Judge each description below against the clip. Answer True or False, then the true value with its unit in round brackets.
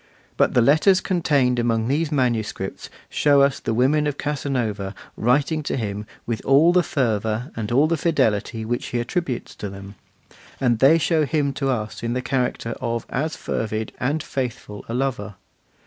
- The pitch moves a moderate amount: True (4.6 semitones)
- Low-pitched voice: True (125 Hz)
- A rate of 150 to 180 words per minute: True (170 wpm)